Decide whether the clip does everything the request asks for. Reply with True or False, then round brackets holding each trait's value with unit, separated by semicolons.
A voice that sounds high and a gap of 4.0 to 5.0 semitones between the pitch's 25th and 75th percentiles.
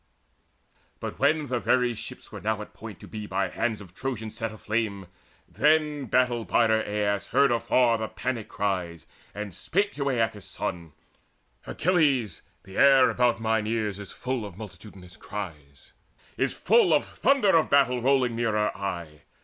False (110 Hz; 4.3 semitones)